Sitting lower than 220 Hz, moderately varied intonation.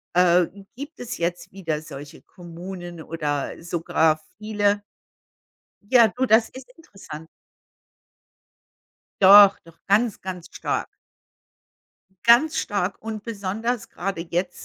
Yes: high, 190 Hz; average, 4.5 semitones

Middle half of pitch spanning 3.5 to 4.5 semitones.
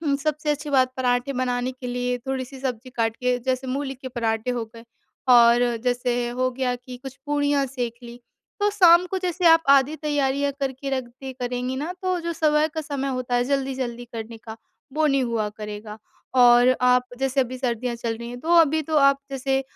No: narrow, 2.5 semitones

